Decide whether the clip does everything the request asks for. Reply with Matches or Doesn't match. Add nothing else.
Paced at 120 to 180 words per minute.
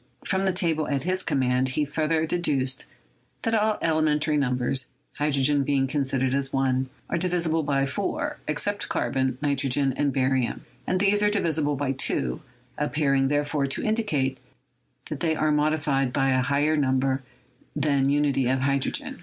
Matches